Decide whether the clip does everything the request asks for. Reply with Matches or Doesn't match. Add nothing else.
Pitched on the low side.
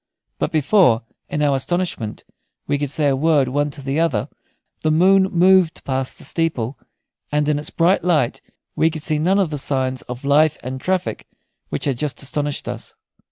Doesn't match